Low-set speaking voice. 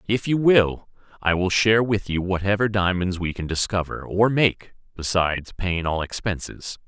Yes: very low, 95 Hz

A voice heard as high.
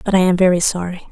No: medium, 180 Hz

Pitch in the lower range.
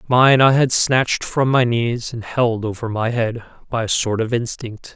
Yes: low, 120 Hz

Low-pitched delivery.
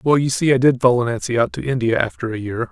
Yes: low, 125 Hz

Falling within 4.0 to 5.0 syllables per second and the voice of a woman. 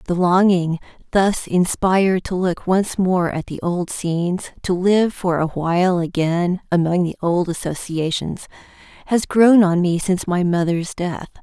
Yes: 4.3 syllables/s; female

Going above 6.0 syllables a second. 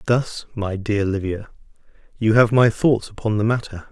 No: 4.7 syllables/s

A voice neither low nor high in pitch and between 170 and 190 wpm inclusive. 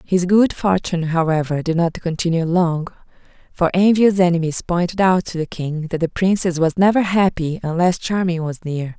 Yes: medium, 175 Hz; average, 175 wpm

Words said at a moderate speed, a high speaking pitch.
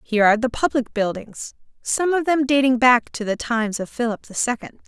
No: fast, 210 wpm; high, 245 Hz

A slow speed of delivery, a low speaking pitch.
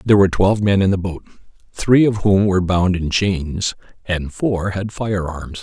No: fast, 205 wpm; very low, 95 Hz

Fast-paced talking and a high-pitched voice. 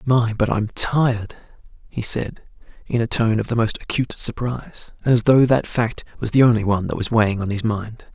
No: fast, 215 wpm; low, 115 Hz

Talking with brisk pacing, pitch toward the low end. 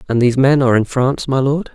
Yes: fast, 275 wpm; low, 130 Hz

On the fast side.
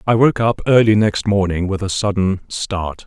No: average, 195 wpm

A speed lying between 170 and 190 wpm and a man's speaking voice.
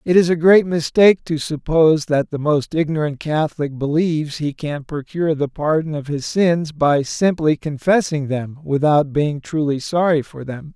Yes: average, 175 wpm; male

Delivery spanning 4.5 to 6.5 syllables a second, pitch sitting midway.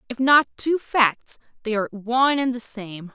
No: 4.6 syllables/s; high, 240 Hz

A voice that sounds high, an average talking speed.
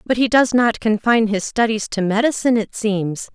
Yes: high, 220 Hz; average, 195 wpm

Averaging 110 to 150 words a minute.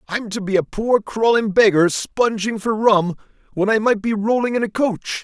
No: fast, 205 wpm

